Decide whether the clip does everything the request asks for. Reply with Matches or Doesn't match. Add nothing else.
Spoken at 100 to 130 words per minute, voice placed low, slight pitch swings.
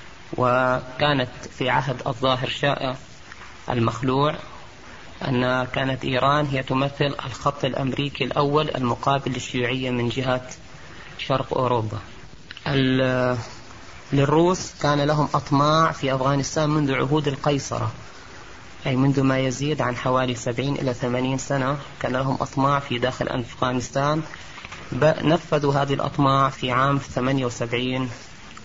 Matches